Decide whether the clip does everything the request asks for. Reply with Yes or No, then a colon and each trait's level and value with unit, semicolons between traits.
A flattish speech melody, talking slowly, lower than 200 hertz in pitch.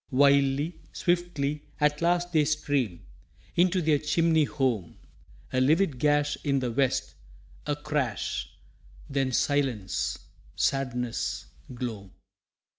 No: average, 3.2 semitones; slow, 105 wpm; medium, 140 Hz